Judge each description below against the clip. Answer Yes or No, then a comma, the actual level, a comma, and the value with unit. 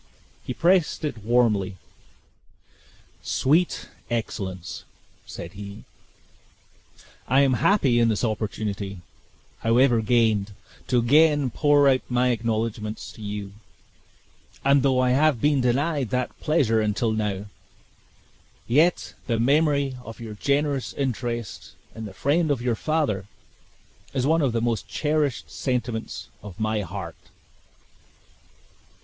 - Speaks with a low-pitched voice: Yes, low, 120 Hz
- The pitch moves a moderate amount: Yes, average, 4.5 semitones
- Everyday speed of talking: No, slow, 120 wpm